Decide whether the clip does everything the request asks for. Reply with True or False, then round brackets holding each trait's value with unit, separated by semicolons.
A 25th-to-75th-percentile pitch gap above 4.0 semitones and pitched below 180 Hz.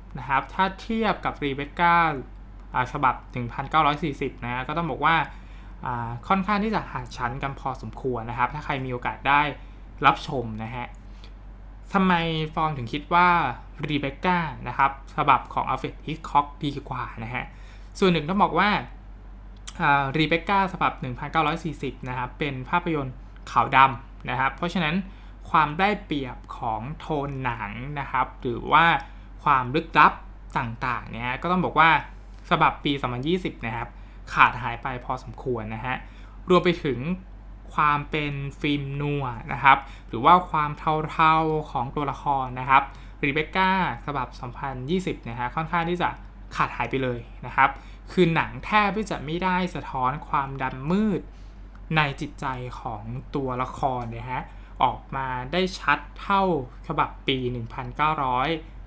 True (4.5 semitones; 135 Hz)